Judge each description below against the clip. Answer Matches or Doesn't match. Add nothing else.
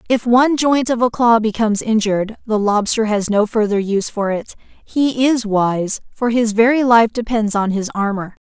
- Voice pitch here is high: Matches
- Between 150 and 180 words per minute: Doesn't match